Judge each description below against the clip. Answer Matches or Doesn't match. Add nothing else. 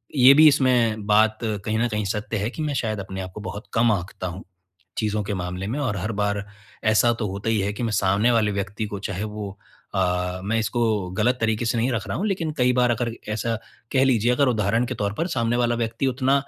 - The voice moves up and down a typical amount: Matches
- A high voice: Doesn't match